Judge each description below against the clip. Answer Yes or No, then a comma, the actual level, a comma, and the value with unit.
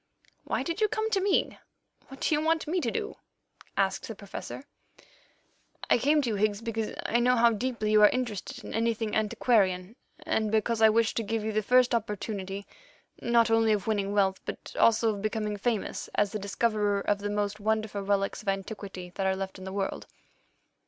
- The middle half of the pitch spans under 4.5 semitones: Yes, narrow, 2.6 semitones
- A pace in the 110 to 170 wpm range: No, average, 195 wpm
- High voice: Yes, high, 215 Hz